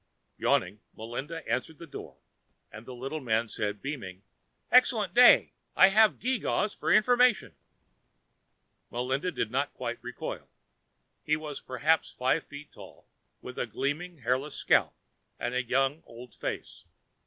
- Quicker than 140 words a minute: No, slow, 135 wpm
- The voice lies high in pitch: No, low, 135 Hz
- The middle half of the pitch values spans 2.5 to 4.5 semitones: No, wide, 5.5 semitones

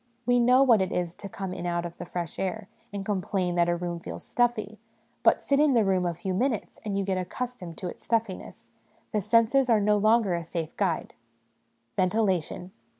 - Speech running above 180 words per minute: Yes, fast, 205 wpm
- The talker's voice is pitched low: No, high, 195 Hz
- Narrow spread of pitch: No, average, 4.1 semitones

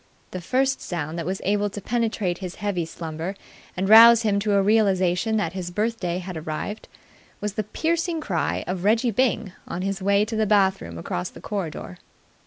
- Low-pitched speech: No, high, 200 Hz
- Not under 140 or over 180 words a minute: No, average, 190 wpm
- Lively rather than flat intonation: No, average, 3.7 semitones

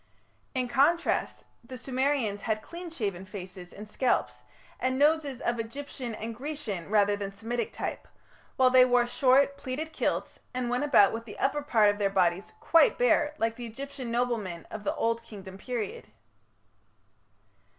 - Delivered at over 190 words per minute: No, average, 160 wpm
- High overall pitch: Yes, high, 240 Hz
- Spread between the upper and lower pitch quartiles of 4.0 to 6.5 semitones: Yes, average, 4.7 semitones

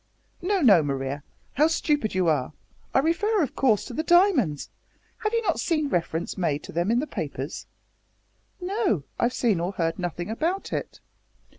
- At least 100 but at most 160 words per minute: No, average, 170 wpm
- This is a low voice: No, high, 240 Hz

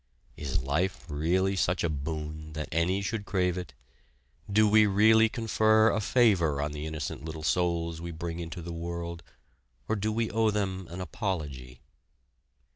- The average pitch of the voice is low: Yes, very low, 85 Hz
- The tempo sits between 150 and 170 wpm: Yes, average, 160 wpm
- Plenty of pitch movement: No, average, 4.5 semitones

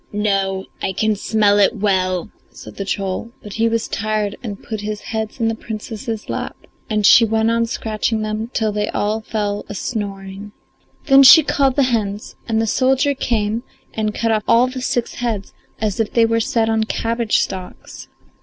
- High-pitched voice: Yes, high, 220 Hz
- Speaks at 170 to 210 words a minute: Yes, average, 185 wpm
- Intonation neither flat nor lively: No, narrow, 1.9 semitones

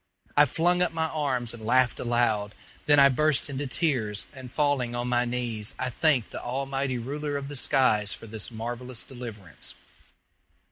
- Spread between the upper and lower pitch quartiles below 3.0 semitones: No, average, 3.3 semitones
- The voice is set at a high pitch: No, low, 125 Hz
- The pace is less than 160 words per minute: No, average, 170 wpm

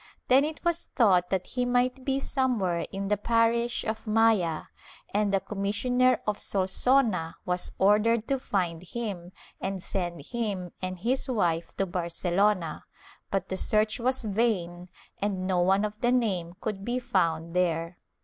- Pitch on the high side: Yes, high, 205 Hz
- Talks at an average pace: Yes, average, 155 wpm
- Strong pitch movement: No, average, 4.8 semitones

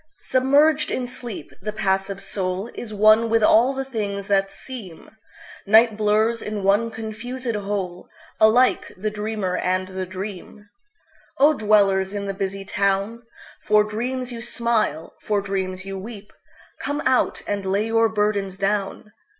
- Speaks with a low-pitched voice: No, high, 210 Hz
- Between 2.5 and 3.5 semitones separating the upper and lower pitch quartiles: Yes, average, 2.8 semitones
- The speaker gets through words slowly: Yes, slow, 125 wpm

